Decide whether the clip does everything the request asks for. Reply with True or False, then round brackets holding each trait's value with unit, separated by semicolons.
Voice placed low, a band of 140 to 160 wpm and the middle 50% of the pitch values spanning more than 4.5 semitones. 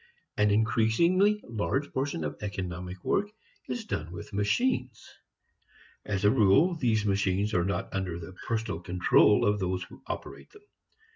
True (105 Hz; 145 wpm; 5.4 semitones)